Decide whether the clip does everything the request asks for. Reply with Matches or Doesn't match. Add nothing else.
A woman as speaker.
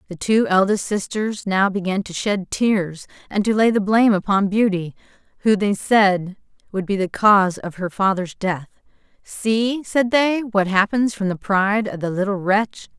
Matches